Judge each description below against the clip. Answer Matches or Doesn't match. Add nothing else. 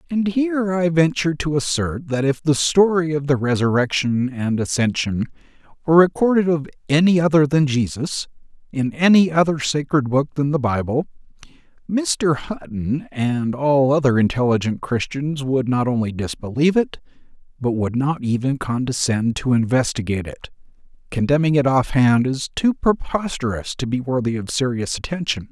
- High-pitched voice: Doesn't match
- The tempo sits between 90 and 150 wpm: Matches